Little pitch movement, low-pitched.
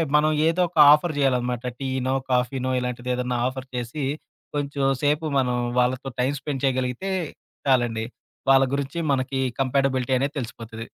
Yes: narrow, 2.1 semitones; low, 130 Hz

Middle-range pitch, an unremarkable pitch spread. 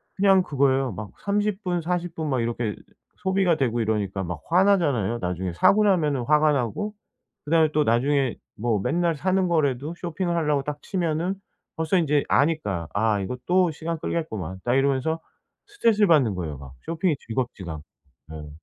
No: medium, 150 Hz; wide, 7.3 semitones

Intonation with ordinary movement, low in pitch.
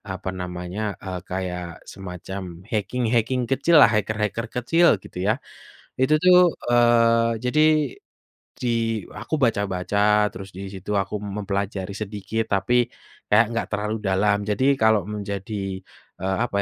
Yes: average, 3.2 semitones; low, 105 Hz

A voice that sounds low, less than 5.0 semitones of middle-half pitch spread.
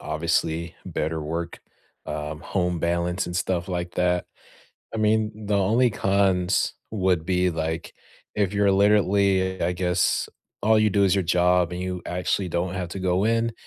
Yes: very low, 90 Hz; narrow, 2.4 semitones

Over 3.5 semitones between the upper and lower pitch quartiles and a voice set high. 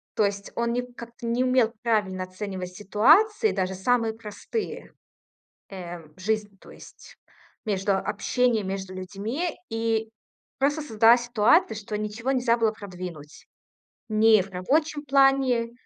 Yes: average, 3.9 semitones; high, 220 Hz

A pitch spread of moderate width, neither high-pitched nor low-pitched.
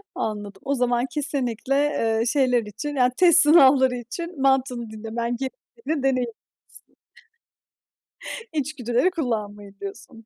No: average, 3.7 semitones; very high, 250 Hz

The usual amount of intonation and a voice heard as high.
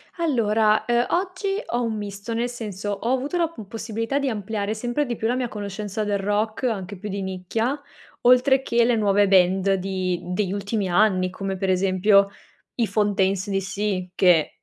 Yes: average, 3.5 semitones; high, 210 Hz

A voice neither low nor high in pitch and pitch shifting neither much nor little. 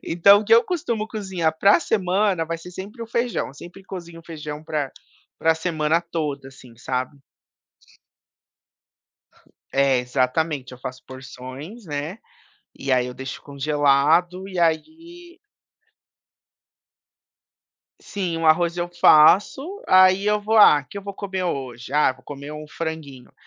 No: medium, 165 Hz; wide, 5.7 semitones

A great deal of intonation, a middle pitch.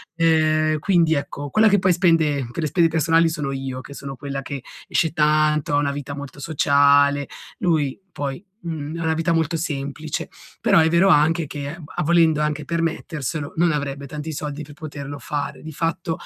No: narrow, 2.4 semitones; medium, 150 Hz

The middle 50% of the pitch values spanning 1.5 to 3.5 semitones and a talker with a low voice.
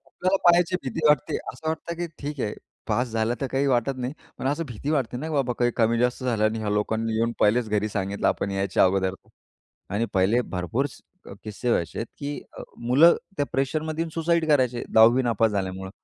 No: average, 5.2 semitones; low, 120 Hz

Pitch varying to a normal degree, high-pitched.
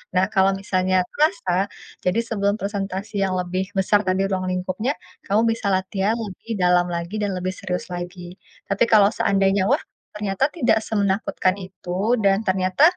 No: narrow, 1.8 semitones; high, 195 Hz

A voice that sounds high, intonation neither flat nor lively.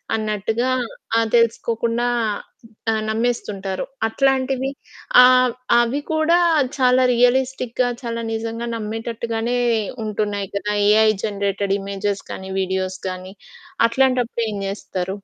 Yes: high, 225 Hz; average, 3.5 semitones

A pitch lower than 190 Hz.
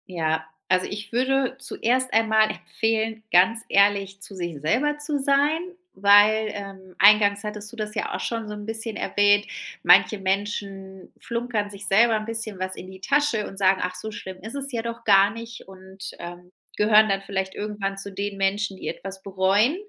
No: high, 205 Hz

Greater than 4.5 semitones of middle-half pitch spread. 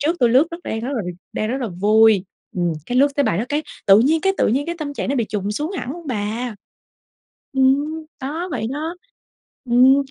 Yes: average, 5.0 semitones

